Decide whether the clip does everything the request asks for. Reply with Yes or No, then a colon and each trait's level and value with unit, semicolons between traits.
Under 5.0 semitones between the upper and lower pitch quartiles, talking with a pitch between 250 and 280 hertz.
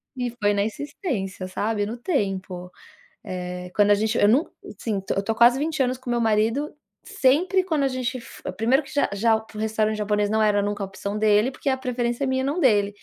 No: average, 4.2 semitones; high, 220 Hz